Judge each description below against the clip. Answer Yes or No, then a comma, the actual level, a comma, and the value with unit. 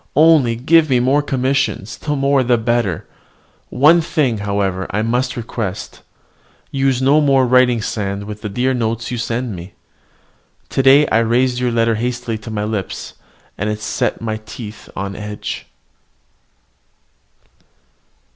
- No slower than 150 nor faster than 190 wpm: No, average, 140 wpm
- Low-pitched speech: Yes, low, 120 Hz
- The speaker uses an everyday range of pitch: Yes, average, 3.6 semitones